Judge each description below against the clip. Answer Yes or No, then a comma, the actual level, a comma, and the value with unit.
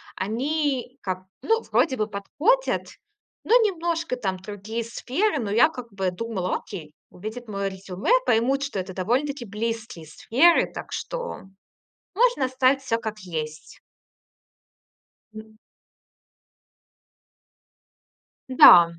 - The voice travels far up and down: Yes, wide, 6.1 semitones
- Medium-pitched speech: No, high, 230 Hz